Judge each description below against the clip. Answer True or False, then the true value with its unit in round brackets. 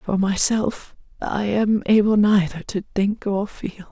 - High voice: True (200 Hz)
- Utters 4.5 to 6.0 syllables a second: False (4.0 syllables/s)